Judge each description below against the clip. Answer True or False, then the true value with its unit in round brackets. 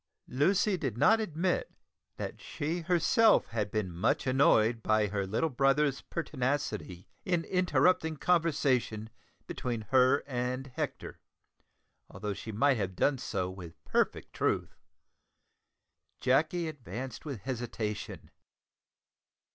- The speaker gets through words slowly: True (110 wpm)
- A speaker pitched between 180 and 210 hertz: False (130 Hz)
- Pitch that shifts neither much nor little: False (6.5 semitones)